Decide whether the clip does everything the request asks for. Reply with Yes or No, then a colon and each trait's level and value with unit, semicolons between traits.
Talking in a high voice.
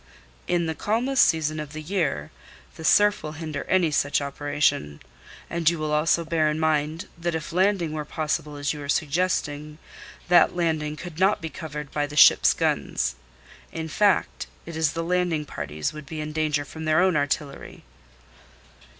No: medium, 155 Hz